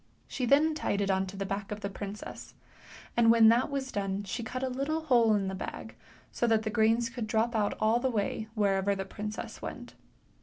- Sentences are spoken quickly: Yes, fast, 220 wpm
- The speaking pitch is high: Yes, high, 220 Hz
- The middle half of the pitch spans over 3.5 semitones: No, average, 3.1 semitones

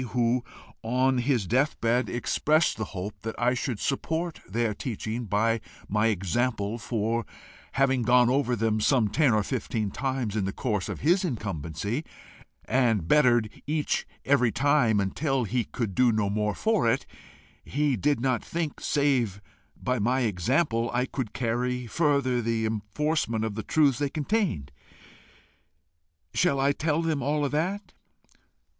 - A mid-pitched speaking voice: No, low, 120 Hz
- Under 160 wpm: Yes, average, 150 wpm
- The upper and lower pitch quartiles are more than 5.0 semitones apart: No, average, 4.3 semitones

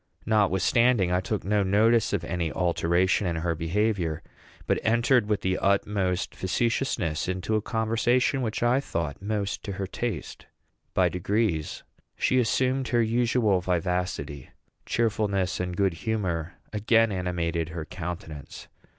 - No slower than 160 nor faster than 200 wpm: No, slow, 135 wpm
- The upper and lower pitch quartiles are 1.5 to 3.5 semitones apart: No, average, 4.2 semitones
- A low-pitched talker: Yes, low, 100 Hz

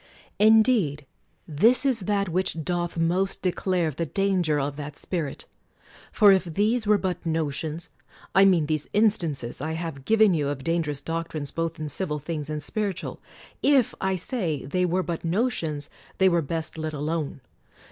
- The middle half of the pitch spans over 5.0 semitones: No, average, 4.1 semitones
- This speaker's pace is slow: No, average, 165 wpm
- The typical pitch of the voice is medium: Yes, medium, 165 Hz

